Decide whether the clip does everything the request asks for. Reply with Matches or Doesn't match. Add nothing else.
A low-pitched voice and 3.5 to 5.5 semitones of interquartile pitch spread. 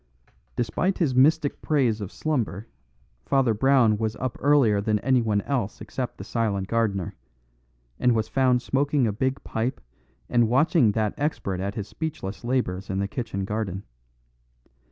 Matches